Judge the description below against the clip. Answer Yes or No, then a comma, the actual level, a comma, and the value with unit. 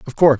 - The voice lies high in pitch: No, medium, 145 Hz